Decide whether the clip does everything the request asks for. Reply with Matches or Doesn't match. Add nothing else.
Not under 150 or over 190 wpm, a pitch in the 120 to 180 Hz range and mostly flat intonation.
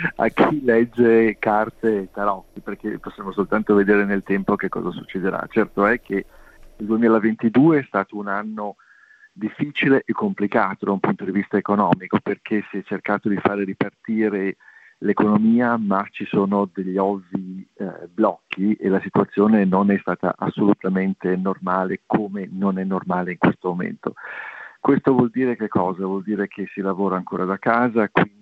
Doesn't match